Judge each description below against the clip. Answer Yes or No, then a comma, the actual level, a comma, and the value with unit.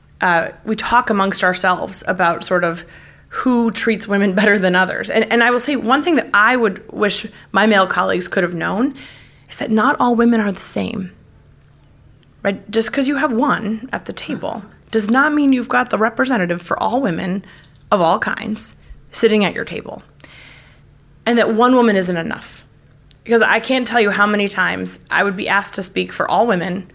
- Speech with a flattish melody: No, average, 5.2 semitones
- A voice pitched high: Yes, high, 205 Hz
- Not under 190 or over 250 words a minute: Yes, average, 195 wpm